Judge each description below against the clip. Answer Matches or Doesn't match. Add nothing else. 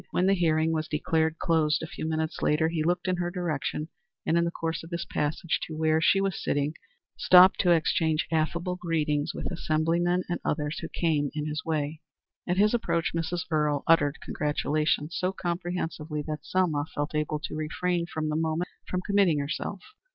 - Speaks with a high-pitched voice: Doesn't match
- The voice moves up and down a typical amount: Doesn't match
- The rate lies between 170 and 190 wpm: Matches